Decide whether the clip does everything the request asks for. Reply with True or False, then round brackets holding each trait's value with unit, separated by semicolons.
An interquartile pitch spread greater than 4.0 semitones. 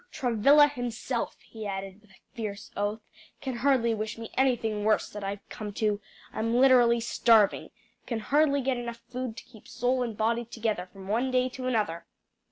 False (3.0 semitones)